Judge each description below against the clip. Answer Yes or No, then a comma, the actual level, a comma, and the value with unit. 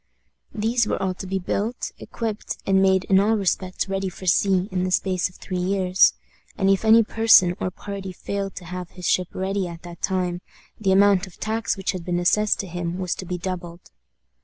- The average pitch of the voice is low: No, high, 190 Hz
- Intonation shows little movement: Yes, narrow, 1.7 semitones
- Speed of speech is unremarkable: No, fast, 210 wpm